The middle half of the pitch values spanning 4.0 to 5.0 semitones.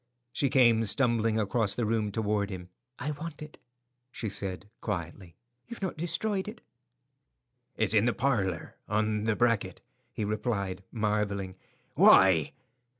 No: average, 3.5 semitones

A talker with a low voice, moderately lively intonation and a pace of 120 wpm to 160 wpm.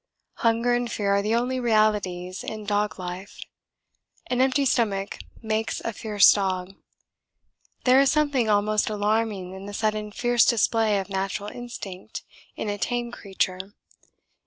No: high, 215 Hz; average, 3.1 semitones; average, 140 wpm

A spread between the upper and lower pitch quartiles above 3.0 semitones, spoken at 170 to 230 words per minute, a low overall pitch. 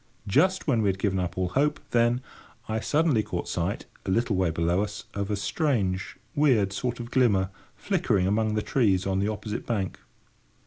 Yes: average, 4.1 semitones; average, 185 wpm; low, 105 Hz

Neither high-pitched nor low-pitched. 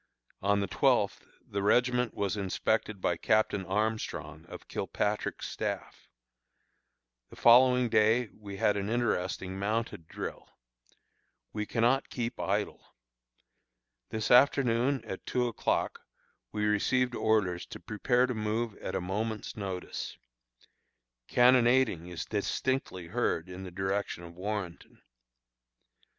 No: low, 105 Hz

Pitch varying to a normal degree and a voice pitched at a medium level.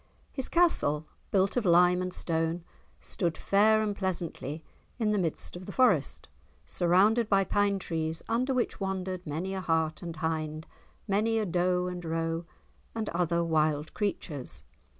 Yes: average, 3.8 semitones; medium, 180 Hz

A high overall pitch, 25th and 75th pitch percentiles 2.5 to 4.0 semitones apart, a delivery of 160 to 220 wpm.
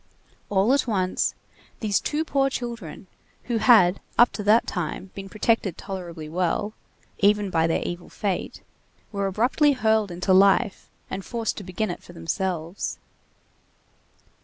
No: high, 200 Hz; average, 3.7 semitones; average, 140 wpm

